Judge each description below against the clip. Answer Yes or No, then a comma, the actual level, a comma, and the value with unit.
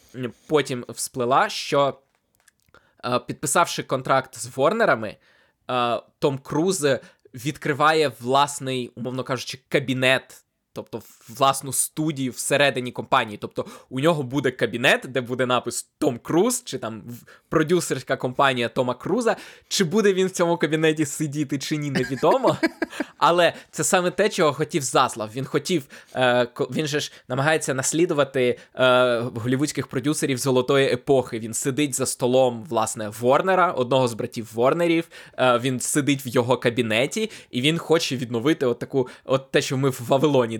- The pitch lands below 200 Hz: Yes, low, 135 Hz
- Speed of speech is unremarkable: Yes, average, 135 wpm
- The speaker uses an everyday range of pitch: Yes, average, 3.6 semitones